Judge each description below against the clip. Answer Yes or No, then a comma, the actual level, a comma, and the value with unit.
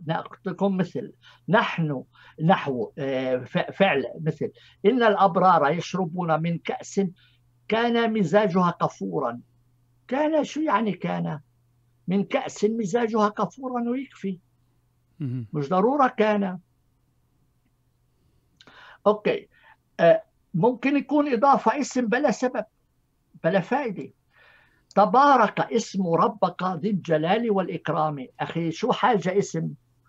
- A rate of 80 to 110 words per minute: Yes, average, 90 wpm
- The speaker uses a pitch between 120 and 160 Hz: No, medium, 185 Hz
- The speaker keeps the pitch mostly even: No, wide, 7.8 semitones